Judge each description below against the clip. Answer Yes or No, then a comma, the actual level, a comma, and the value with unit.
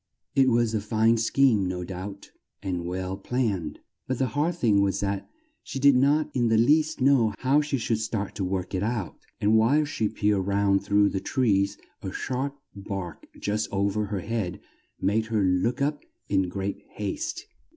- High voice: No, low, 105 Hz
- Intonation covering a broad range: No, average, 4.6 semitones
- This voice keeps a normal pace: Yes, average, 180 wpm